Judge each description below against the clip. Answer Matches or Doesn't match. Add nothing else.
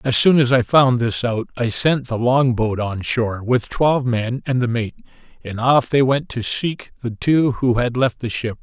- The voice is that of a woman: Doesn't match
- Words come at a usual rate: Doesn't match